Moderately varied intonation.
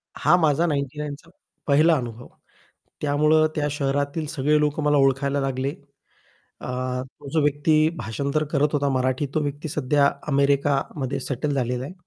No: narrow, 1.7 semitones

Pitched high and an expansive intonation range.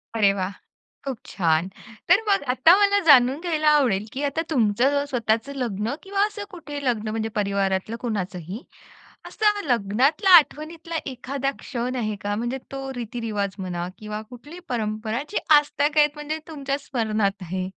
Yes: high, 245 Hz; wide, 5.8 semitones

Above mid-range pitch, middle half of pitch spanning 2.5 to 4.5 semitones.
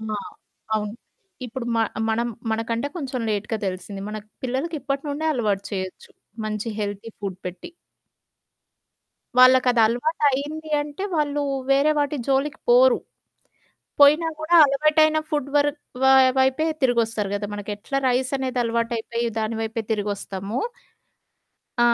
No: high, 245 Hz; average, 5.1 semitones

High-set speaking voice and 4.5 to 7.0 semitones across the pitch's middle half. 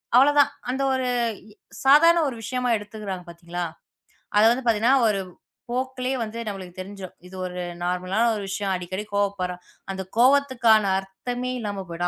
Yes: high, 210 Hz; average, 5.0 semitones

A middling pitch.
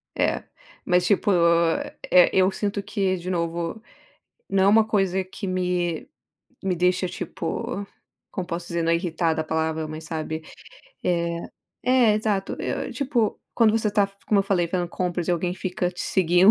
Yes: medium, 180 Hz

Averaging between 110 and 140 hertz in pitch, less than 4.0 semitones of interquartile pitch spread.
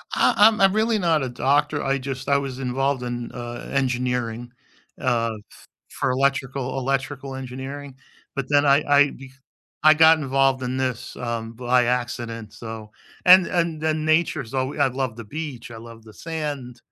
Yes: low, 135 Hz; average, 2.9 semitones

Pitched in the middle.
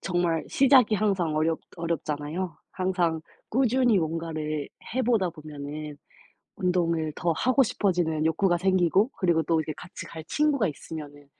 Yes: medium, 170 Hz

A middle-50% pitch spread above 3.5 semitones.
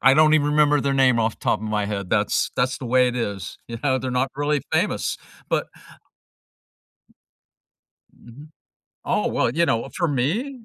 Yes: average, 4.0 semitones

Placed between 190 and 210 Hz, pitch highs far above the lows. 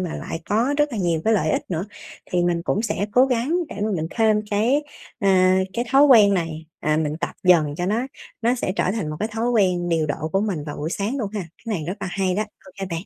No: high, 195 Hz; average, 4.8 semitones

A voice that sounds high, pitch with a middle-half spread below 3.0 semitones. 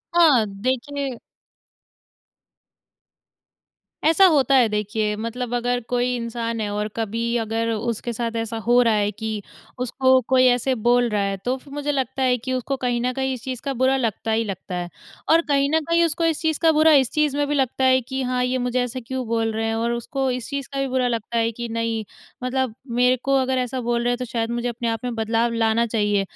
Yes: high, 245 Hz; narrow, 2.5 semitones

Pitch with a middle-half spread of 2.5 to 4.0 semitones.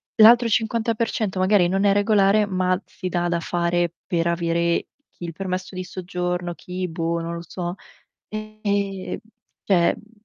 Yes: average, 2.9 semitones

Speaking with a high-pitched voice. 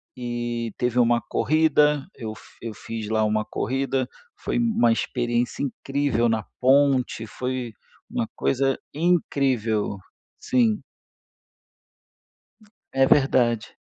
No: low, 125 Hz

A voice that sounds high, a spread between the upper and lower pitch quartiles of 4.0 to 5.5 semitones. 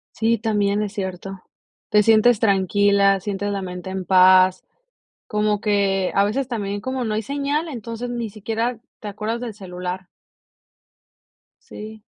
No: high, 205 Hz; narrow, 2.6 semitones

